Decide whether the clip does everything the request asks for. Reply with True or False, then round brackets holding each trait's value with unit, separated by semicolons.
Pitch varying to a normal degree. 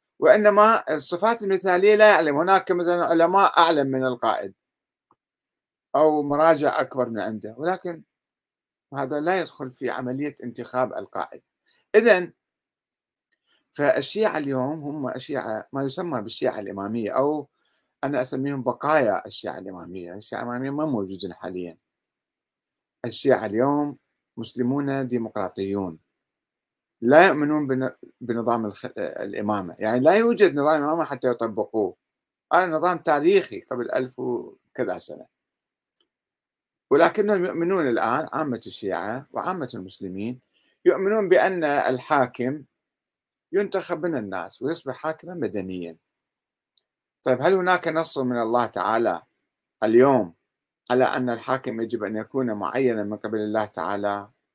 False (6.9 semitones)